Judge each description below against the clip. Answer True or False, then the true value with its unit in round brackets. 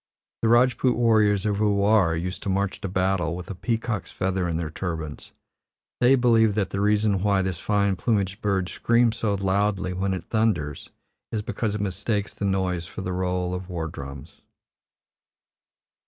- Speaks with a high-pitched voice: False (100 Hz)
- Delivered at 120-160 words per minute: False (170 wpm)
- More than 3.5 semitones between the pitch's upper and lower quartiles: False (2.8 semitones)